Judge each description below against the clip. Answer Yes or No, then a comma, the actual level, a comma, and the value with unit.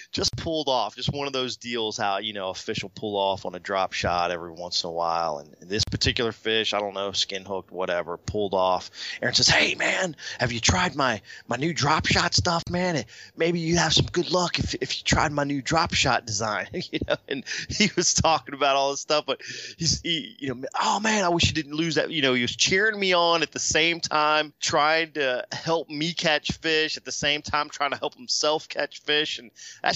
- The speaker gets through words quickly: Yes, fast, 235 wpm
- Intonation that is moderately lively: No, wide, 7.2 semitones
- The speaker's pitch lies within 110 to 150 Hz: Yes, medium, 140 Hz